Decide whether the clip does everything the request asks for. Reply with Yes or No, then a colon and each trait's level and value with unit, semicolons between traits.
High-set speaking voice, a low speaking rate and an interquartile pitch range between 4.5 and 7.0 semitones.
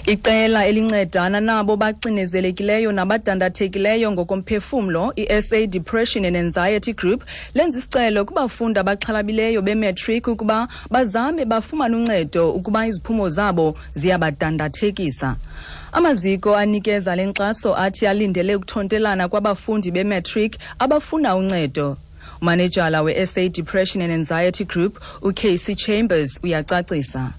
No: high, 205 Hz; slow, 95 wpm; average, 3.3 semitones